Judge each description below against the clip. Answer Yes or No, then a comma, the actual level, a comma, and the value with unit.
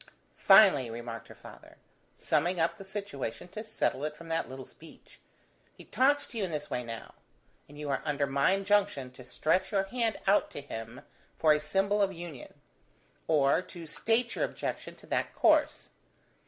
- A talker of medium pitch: Yes, medium, 165 Hz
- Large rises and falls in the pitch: Yes, wide, 5.9 semitones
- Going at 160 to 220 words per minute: Yes, average, 180 wpm